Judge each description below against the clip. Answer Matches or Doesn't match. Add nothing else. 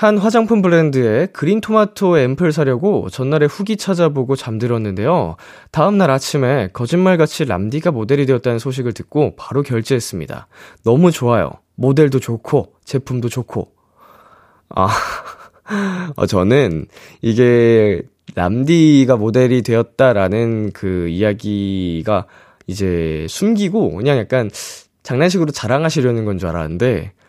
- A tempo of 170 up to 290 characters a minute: Matches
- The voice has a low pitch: Matches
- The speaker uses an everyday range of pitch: Doesn't match